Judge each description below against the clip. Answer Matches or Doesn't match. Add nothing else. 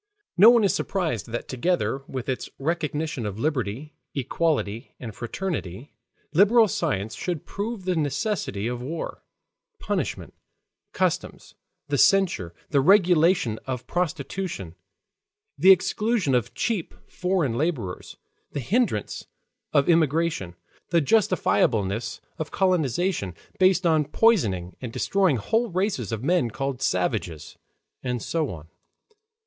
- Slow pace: Matches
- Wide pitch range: Matches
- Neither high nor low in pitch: Matches